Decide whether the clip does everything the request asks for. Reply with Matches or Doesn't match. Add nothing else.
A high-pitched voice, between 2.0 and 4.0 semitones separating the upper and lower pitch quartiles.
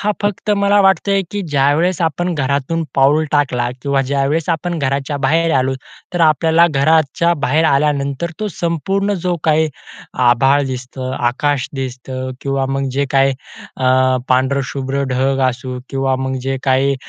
Doesn't match